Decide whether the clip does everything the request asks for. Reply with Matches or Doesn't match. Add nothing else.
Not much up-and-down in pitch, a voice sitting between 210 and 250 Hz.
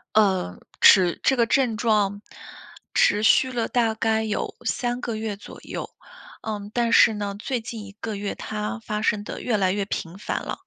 Matches